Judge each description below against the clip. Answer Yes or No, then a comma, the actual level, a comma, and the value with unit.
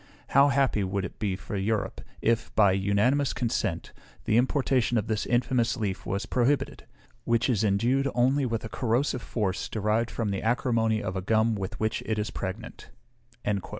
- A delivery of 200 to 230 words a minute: No, average, 170 wpm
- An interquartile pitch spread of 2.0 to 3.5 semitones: Yes, average, 3.2 semitones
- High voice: No, low, 115 Hz